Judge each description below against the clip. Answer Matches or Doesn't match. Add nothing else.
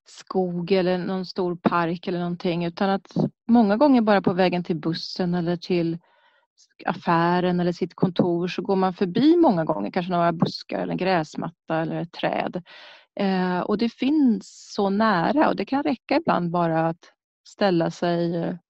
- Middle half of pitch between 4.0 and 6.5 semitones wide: Doesn't match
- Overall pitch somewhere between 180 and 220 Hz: Matches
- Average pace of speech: Matches